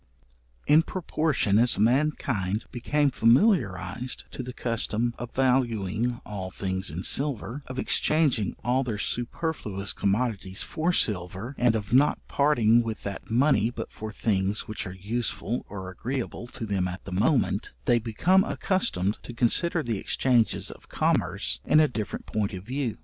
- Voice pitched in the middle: No, low, 115 Hz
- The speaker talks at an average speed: Yes, average, 150 wpm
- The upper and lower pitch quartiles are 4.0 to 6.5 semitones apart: Yes, average, 4.6 semitones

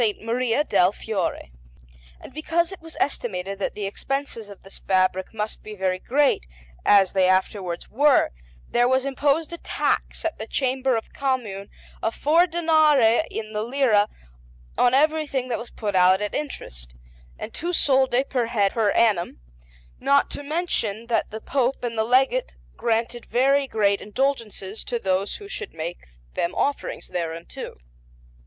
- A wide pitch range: Yes, wide, 5.7 semitones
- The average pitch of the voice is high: Yes, high, 235 Hz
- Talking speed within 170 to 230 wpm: No, average, 160 wpm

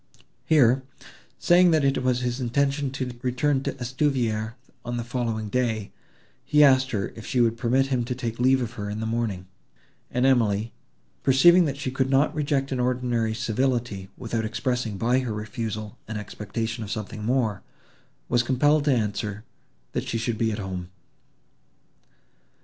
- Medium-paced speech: Yes, average, 165 wpm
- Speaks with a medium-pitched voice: No, low, 120 Hz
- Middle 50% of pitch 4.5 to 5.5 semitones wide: No, average, 3.1 semitones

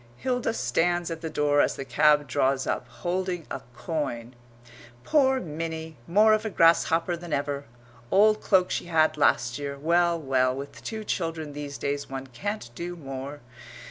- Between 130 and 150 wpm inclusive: No, average, 165 wpm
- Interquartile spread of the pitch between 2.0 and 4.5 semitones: Yes, average, 3.8 semitones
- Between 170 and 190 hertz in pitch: No, medium, 160 Hz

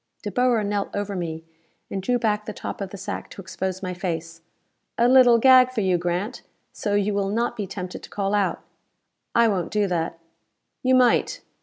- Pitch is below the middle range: No, high, 205 Hz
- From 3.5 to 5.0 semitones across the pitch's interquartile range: Yes, average, 3.9 semitones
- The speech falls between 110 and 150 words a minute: No, average, 195 wpm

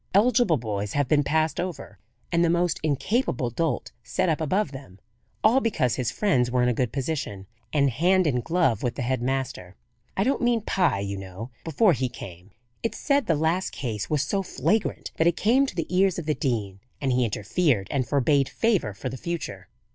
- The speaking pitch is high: No, medium, 145 Hz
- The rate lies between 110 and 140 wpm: No, average, 200 wpm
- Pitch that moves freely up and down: Yes, wide, 6.7 semitones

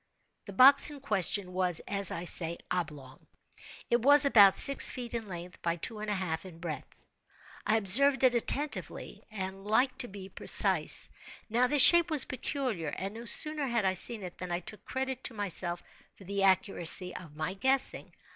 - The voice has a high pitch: Yes, high, 200 Hz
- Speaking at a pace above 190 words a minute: No, average, 185 wpm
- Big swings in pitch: Yes, wide, 5.9 semitones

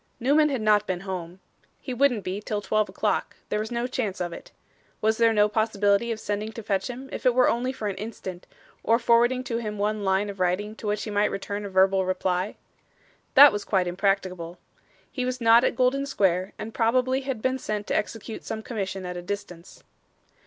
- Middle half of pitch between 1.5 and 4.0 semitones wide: Yes, average, 3.5 semitones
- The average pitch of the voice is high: Yes, high, 210 Hz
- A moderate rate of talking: No, fast, 210 wpm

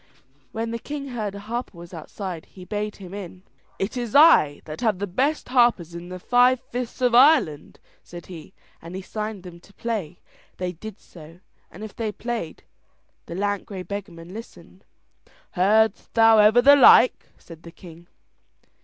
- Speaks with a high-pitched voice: Yes, high, 205 Hz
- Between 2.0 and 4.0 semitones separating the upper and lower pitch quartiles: No, average, 4.9 semitones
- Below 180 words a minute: Yes, average, 170 wpm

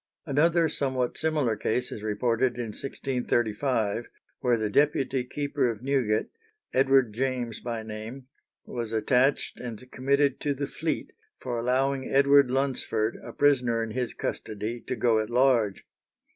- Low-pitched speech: Yes, low, 125 Hz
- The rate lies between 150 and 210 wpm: No, average, 140 wpm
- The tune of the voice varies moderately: Yes, average, 3.2 semitones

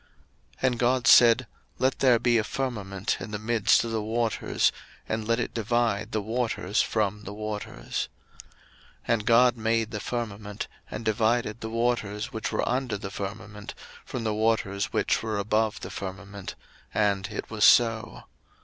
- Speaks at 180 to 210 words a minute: No, average, 165 wpm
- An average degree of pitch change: No, narrow, 2.2 semitones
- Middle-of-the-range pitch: No, low, 110 Hz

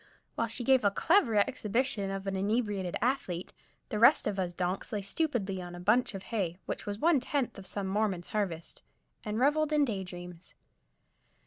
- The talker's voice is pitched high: Yes, high, 205 Hz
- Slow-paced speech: No, average, 185 wpm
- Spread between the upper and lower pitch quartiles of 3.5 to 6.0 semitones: Yes, average, 4.4 semitones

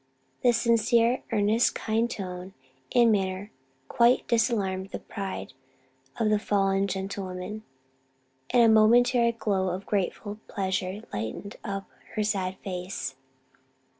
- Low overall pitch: No, high, 205 Hz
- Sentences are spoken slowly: Yes, slow, 115 wpm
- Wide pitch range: No, average, 3.3 semitones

